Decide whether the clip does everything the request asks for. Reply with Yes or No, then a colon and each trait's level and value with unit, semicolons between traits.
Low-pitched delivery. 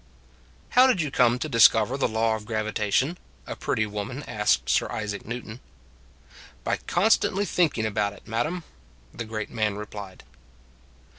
Yes: low, 110 Hz